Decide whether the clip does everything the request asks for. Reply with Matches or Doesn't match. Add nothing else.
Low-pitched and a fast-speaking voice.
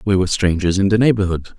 Matches